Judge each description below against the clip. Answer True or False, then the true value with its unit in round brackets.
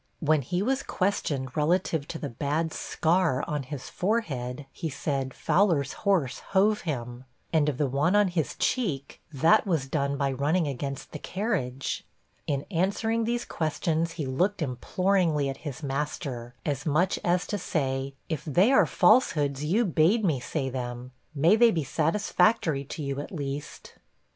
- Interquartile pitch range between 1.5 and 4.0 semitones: False (5.0 semitones)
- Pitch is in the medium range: True (155 Hz)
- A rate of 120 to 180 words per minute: True (160 wpm)